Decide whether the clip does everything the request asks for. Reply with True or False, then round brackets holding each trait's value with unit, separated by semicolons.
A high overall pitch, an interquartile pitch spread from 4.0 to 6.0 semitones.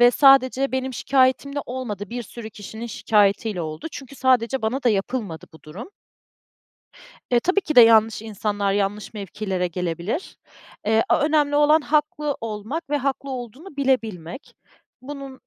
True (240 Hz; 4.8 semitones)